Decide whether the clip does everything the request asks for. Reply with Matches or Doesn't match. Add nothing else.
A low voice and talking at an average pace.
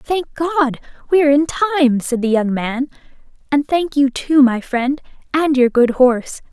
Doesn't match